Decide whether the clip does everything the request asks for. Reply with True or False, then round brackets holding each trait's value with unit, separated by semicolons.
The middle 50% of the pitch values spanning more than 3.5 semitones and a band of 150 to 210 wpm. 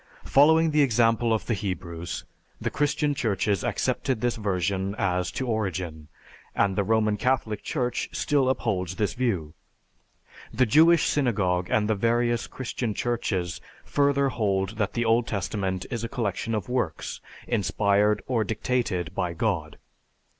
False (4.3 semitones; 140 wpm)